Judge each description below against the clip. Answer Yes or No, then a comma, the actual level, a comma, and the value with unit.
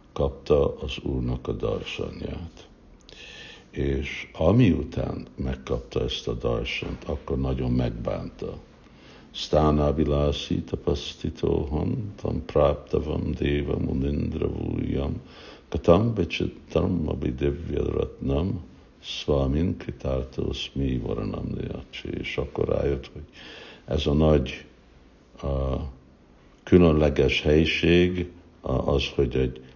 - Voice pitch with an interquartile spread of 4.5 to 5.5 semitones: No, average, 3.7 semitones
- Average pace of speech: No, slow, 85 wpm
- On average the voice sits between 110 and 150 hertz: No, very low, 70 Hz